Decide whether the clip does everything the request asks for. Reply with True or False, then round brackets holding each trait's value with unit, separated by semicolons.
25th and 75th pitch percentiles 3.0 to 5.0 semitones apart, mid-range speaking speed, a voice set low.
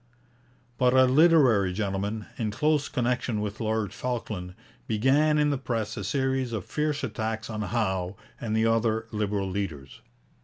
True (4.0 semitones; 150 wpm; 110 Hz)